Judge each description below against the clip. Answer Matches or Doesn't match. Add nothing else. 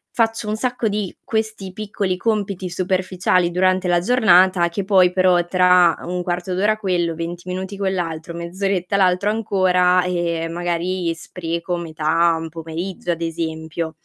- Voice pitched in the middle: Matches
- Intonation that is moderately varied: Doesn't match